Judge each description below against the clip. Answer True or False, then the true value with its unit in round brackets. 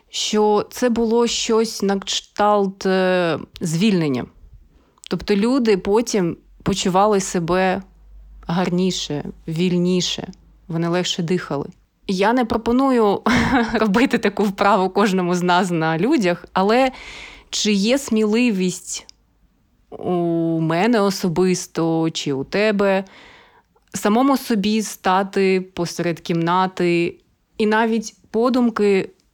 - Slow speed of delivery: True (95 wpm)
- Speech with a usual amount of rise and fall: True (3.6 semitones)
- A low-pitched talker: False (195 Hz)